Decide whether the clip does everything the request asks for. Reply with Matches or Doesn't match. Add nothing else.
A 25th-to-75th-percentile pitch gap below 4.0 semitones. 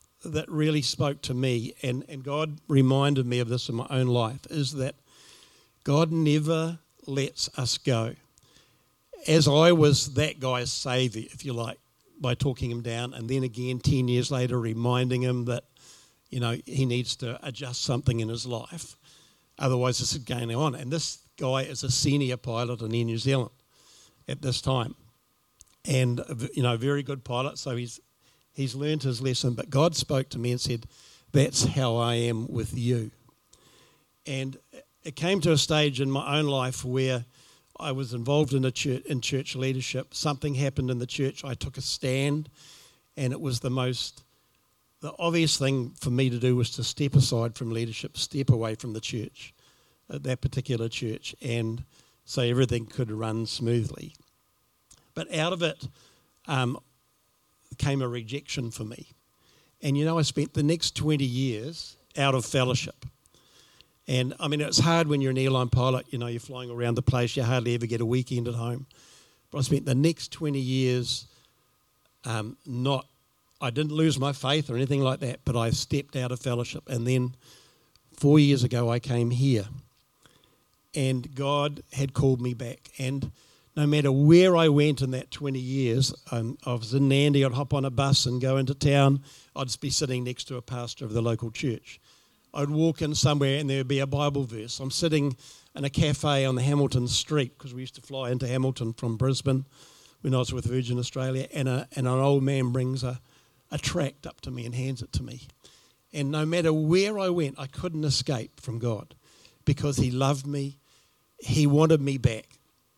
Matches